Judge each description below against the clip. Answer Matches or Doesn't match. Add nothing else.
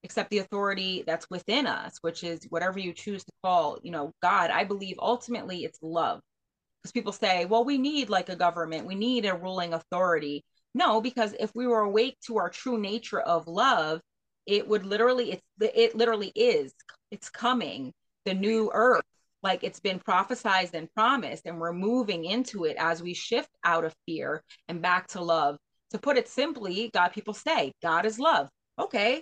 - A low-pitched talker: Doesn't match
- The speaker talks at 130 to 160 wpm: Doesn't match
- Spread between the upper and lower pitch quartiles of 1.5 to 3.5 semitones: Doesn't match